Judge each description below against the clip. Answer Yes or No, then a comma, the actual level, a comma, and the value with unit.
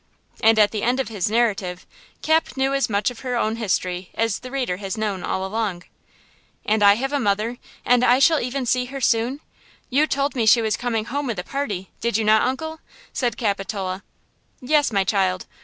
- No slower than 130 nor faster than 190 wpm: No, average, 200 wpm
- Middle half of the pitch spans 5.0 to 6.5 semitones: No, average, 4.3 semitones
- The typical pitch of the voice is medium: No, high, 225 Hz